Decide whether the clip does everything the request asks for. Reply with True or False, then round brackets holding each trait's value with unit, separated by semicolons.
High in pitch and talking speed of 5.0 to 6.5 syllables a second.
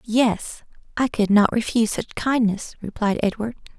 False (220 Hz; 4.6 syllables/s)